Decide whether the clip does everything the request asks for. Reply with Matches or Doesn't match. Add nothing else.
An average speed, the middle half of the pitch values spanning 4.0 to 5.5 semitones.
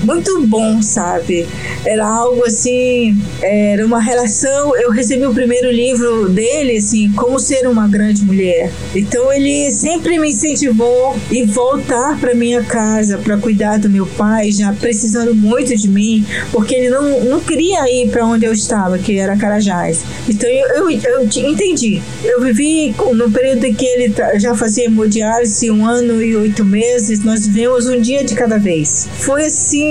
Doesn't match